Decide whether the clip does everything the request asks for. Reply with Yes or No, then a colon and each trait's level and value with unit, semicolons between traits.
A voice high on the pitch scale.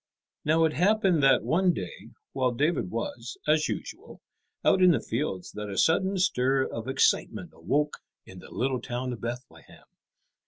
No: low, 135 Hz